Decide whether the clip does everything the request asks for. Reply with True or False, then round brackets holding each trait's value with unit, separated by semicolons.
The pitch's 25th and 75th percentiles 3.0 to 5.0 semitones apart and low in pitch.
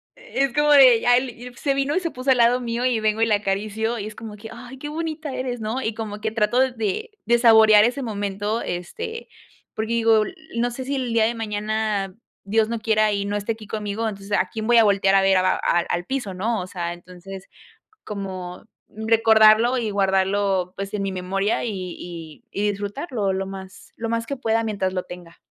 False (3.4 semitones; 215 Hz)